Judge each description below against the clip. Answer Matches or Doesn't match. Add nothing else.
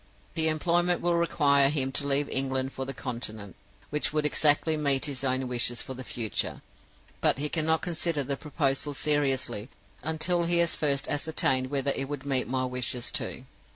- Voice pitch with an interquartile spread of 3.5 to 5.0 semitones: Doesn't match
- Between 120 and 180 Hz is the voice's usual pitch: Matches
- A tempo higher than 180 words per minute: Doesn't match